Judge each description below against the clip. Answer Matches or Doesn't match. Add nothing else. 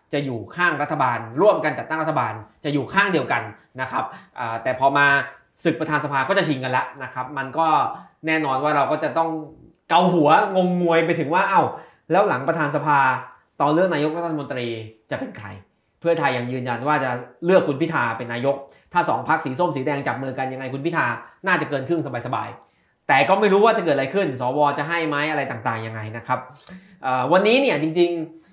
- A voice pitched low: Doesn't match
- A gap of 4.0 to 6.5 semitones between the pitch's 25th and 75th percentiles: Matches